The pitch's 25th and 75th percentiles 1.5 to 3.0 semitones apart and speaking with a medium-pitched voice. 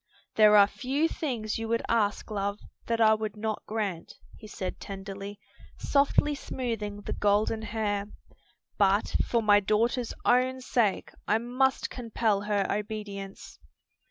No: narrow, 2.4 semitones; high, 215 Hz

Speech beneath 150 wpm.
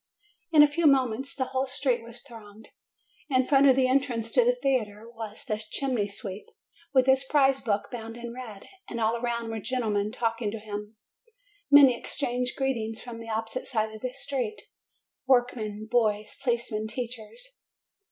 No: average, 170 wpm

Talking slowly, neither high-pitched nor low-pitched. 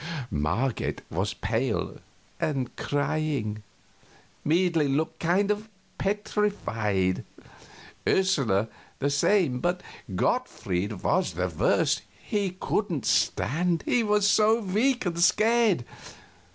Yes: slow, 100 wpm; medium, 165 Hz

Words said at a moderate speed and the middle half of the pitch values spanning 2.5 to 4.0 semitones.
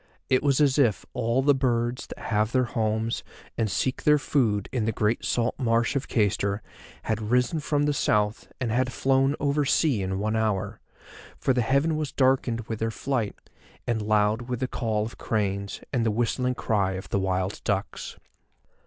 Yes: average, 185 wpm; average, 3.7 semitones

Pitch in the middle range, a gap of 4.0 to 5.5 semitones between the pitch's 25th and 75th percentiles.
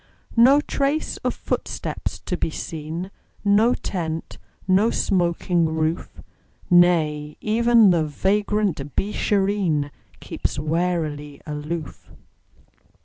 Yes: medium, 175 Hz; average, 4.7 semitones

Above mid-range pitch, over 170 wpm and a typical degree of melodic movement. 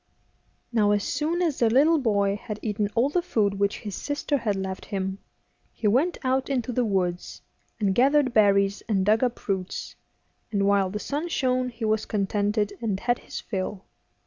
Yes: high, 215 Hz; average, 180 wpm; average, 4.3 semitones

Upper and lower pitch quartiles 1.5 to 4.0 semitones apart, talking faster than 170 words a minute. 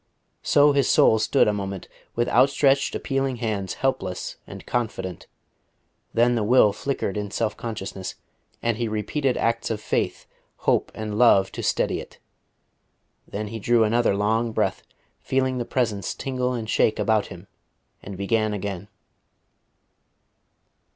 No: average, 3.1 semitones; average, 140 wpm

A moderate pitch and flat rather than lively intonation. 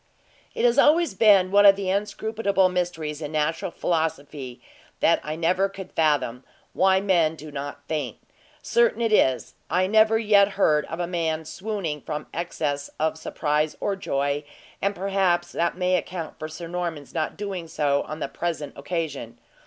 No: medium, 170 Hz; average, 4.4 semitones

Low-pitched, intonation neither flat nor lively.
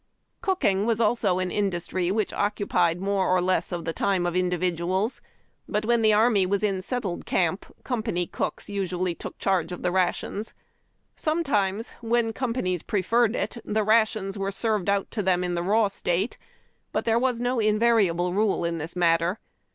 No: high, 195 Hz; average, 3.7 semitones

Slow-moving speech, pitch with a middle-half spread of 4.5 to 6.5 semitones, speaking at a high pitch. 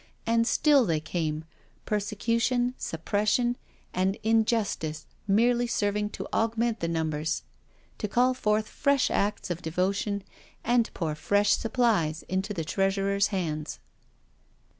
Yes: slow, 120 wpm; average, 5.2 semitones; high, 205 Hz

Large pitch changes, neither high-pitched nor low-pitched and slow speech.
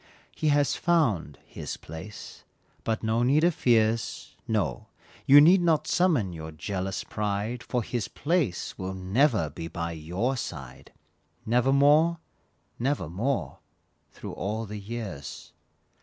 No: wide, 7.0 semitones; low, 110 Hz; slow, 125 wpm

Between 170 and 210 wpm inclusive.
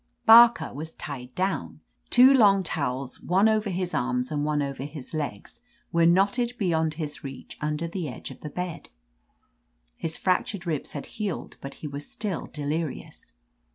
No: average, 160 wpm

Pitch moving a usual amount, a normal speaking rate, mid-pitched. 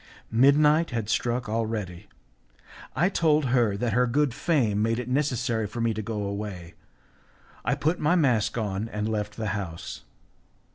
No: average, 4.7 semitones; average, 155 wpm; low, 115 Hz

